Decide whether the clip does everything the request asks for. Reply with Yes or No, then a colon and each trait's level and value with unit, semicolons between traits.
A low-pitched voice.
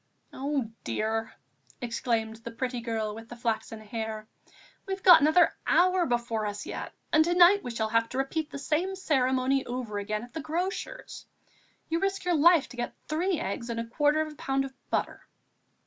No: very high, 255 Hz